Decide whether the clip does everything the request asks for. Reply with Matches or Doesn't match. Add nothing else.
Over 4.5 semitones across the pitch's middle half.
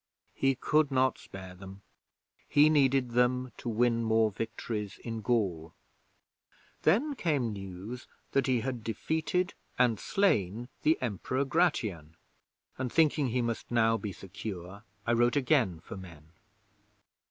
Matches